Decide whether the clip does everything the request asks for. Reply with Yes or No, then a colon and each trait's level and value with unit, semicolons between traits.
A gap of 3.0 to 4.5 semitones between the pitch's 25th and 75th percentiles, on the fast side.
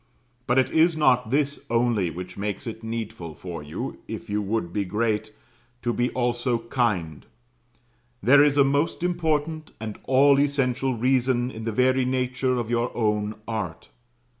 No: average, 3.8 semitones; average, 160 wpm